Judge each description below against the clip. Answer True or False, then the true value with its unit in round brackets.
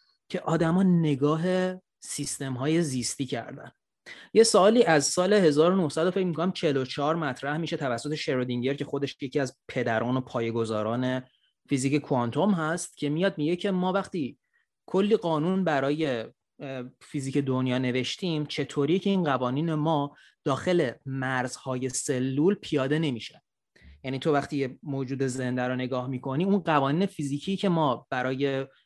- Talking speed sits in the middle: True (135 wpm)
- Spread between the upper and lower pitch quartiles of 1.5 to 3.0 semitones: False (4.3 semitones)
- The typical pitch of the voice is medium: True (145 Hz)